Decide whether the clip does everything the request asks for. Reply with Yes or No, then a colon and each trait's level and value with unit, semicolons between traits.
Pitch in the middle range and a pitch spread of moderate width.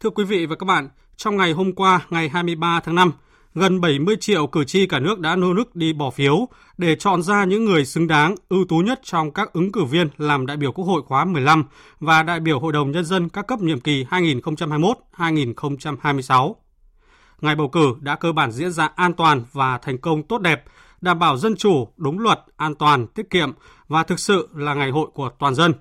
Yes: medium, 165 Hz; average, 3.9 semitones